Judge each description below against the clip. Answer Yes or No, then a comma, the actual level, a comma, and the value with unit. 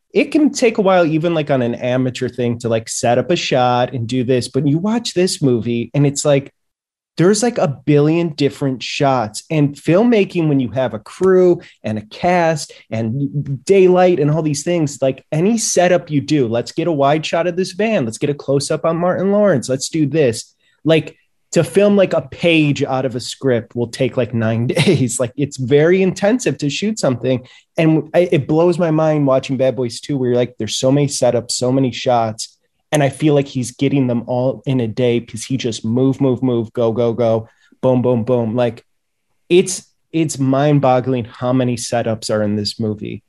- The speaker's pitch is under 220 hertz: Yes, low, 135 Hz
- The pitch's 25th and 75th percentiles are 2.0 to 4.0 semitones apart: No, average, 4.9 semitones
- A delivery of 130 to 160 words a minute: No, fast, 205 wpm